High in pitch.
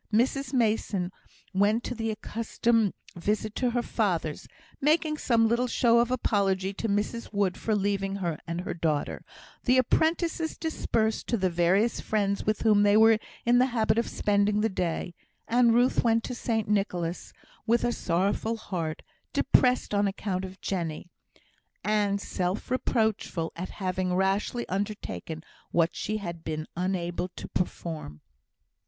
Yes: high, 205 Hz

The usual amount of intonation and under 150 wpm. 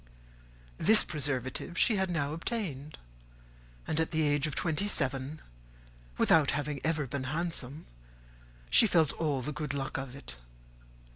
Yes: average, 3.2 semitones; average, 140 wpm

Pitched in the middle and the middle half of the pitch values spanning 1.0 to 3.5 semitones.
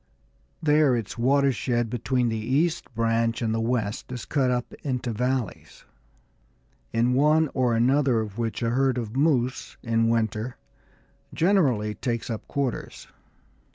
No: low, 125 Hz; average, 2.8 semitones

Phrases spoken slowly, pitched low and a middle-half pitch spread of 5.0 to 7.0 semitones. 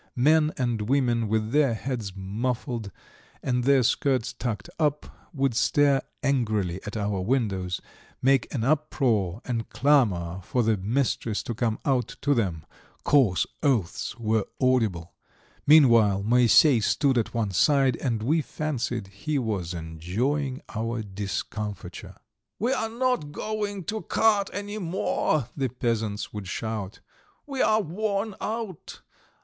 Yes: slow, 130 wpm; low, 120 Hz; wide, 5.5 semitones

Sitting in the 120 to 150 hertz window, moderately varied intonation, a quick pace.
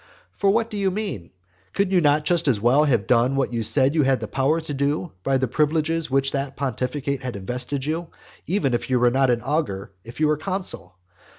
Yes: medium, 140 Hz; average, 4.1 semitones; fast, 230 wpm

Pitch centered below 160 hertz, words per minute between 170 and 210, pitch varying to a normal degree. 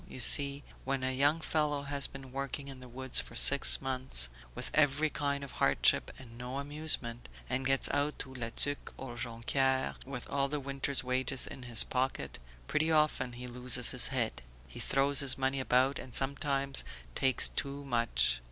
No: low, 135 Hz; average, 180 wpm; narrow, 1.8 semitones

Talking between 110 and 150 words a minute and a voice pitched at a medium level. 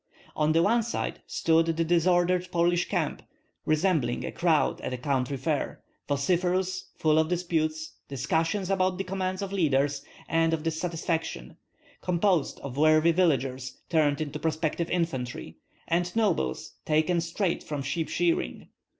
Yes: slow, 135 wpm; medium, 165 Hz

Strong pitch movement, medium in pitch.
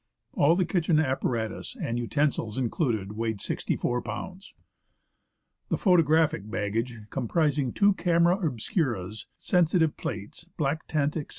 Yes: wide, 6.4 semitones; medium, 145 Hz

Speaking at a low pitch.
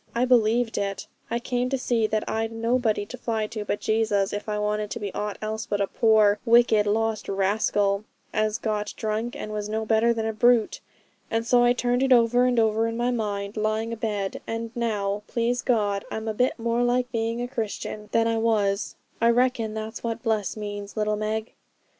No: high, 220 Hz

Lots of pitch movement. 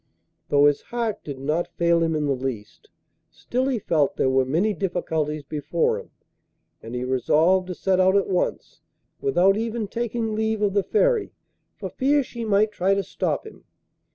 Yes: wide, 6.5 semitones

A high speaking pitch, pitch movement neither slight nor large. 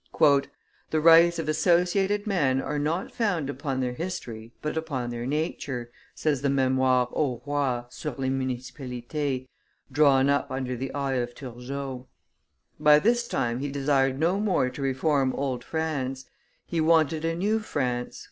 No: medium, 140 Hz; average, 3.6 semitones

